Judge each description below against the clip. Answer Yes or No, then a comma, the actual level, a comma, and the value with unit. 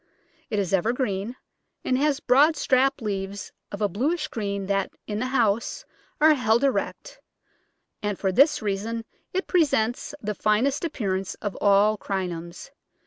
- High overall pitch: Yes, high, 220 Hz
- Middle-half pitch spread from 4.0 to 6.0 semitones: Yes, average, 5.2 semitones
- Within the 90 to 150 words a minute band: Yes, average, 140 wpm